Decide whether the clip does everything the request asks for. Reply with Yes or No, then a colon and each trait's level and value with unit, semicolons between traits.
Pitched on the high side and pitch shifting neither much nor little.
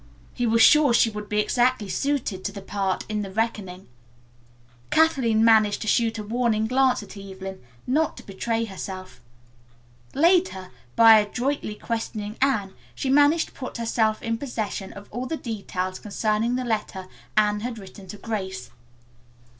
Yes: high, 220 Hz; average, 3.4 semitones